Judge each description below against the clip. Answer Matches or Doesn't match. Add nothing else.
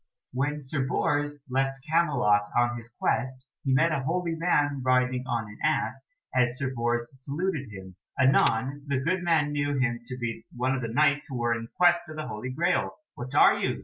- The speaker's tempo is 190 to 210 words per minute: Matches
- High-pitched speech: Doesn't match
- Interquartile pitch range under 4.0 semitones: Matches